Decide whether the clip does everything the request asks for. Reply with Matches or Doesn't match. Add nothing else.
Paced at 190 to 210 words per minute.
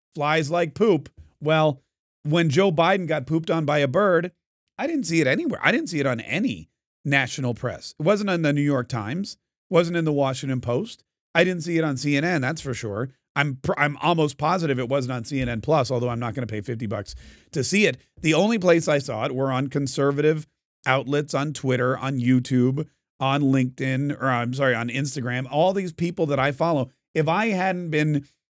Matches